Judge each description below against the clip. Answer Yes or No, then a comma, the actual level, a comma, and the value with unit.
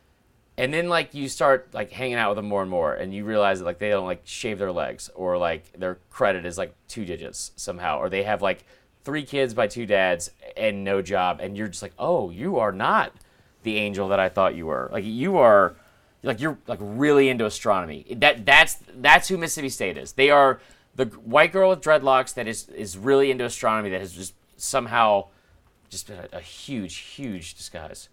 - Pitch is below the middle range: Yes, low, 110 Hz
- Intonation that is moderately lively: No, wide, 6.0 semitones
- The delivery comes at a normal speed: No, fast, 215 wpm